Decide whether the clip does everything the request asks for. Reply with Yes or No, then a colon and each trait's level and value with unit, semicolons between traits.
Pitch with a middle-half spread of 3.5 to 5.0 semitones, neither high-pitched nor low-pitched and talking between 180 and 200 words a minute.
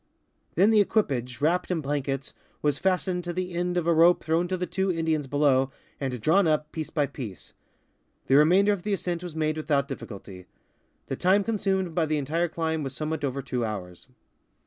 Yes: average, 4.4 semitones; medium, 160 Hz; average, 190 wpm